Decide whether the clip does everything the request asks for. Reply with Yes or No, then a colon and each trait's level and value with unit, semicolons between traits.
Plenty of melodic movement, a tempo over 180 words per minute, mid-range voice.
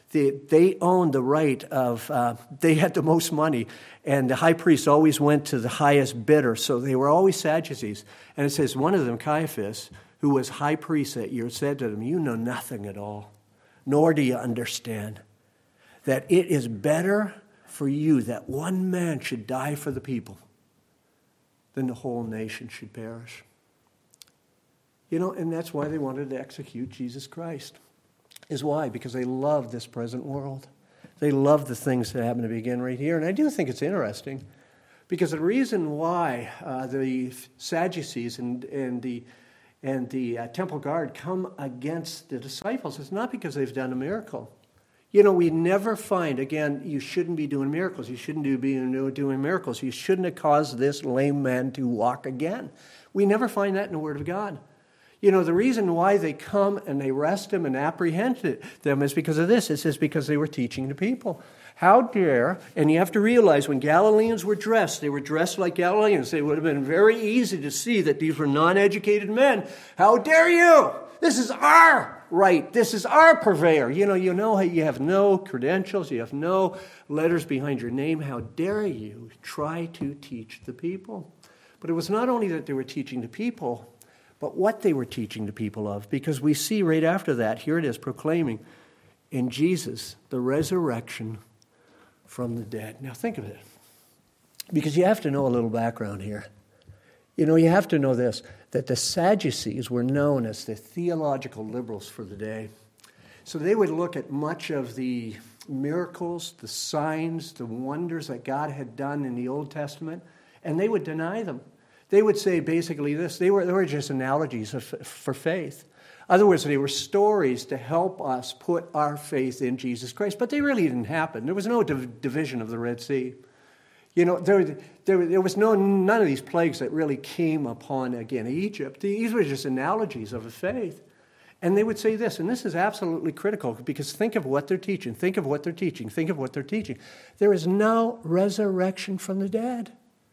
Yes: wide, 6.0 semitones; average, 190 wpm; medium, 150 Hz